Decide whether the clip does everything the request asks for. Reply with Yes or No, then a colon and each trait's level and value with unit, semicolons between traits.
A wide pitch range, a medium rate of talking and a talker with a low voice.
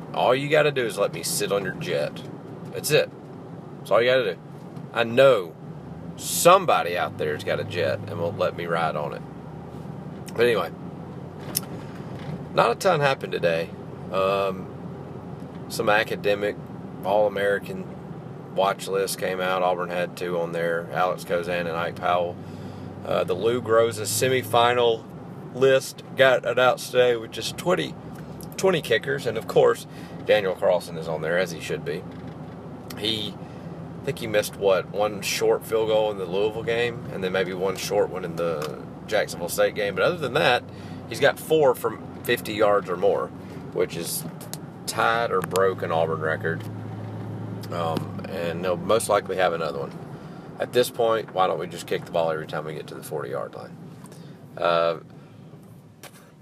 Yes: wide, 8.3 semitones; average, 170 wpm; low, 115 Hz